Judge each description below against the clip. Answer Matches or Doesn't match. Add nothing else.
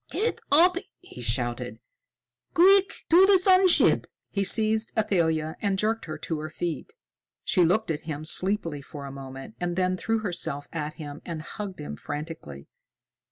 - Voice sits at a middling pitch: Matches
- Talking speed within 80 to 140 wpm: Doesn't match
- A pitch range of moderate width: Doesn't match